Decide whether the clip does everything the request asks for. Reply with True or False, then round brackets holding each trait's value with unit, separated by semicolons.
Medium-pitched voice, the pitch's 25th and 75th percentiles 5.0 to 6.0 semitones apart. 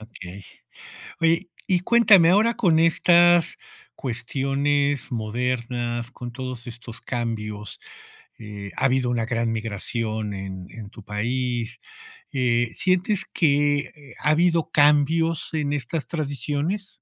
False (130 Hz; 5.5 semitones)